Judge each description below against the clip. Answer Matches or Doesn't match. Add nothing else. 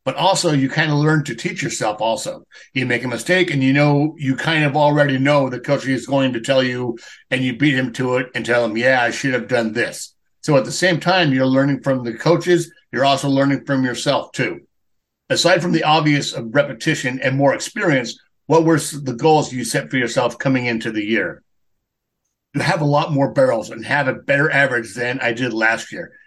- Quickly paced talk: Matches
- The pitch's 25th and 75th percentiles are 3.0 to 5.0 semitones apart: Matches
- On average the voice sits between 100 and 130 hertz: Doesn't match